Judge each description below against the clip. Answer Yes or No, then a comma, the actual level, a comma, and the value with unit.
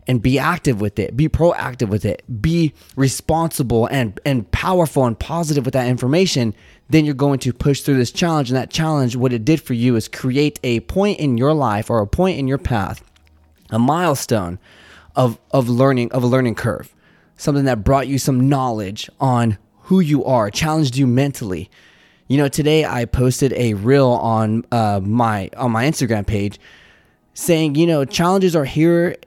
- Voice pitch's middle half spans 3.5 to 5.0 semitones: Yes, average, 4.7 semitones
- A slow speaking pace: No, average, 185 wpm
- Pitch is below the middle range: Yes, low, 130 Hz